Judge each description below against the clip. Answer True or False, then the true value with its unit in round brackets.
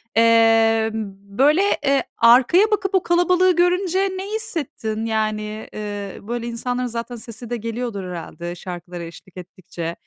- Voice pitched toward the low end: False (230 Hz)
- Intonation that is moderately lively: False (7.2 semitones)